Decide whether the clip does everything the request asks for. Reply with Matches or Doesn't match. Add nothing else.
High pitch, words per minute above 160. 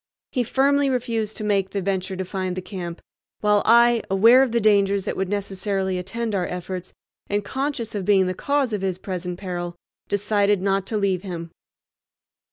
Matches